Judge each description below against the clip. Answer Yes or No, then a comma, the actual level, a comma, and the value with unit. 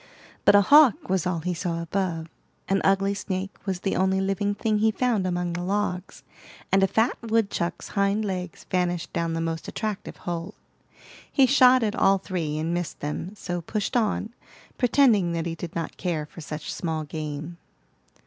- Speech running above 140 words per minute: Yes, average, 175 wpm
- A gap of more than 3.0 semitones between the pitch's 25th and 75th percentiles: Yes, average, 3.5 semitones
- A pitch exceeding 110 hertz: Yes, medium, 185 Hz